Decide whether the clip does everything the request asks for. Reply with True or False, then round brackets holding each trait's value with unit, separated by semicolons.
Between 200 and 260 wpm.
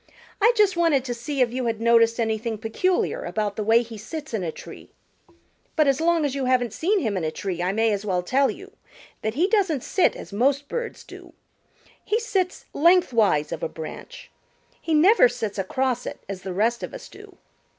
True (205 wpm)